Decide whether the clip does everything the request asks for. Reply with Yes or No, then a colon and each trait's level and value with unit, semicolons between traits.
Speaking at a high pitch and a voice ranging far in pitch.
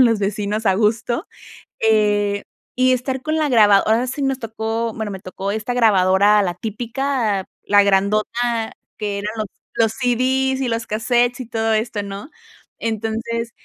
No: high, 225 Hz; average, 2.8 semitones